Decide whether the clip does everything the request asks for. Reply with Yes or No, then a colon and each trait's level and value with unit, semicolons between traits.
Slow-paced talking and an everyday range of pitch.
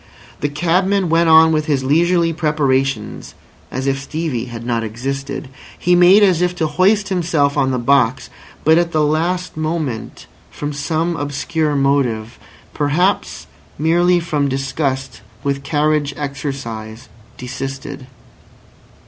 Yes: slow, 130 wpm; average, 3.6 semitones